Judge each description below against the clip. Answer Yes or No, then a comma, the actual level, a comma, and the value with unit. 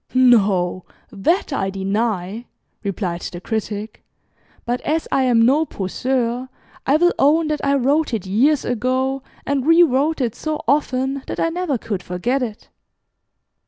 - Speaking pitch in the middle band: No, very high, 250 Hz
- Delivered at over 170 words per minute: No, average, 145 wpm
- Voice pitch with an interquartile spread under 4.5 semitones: No, average, 5.3 semitones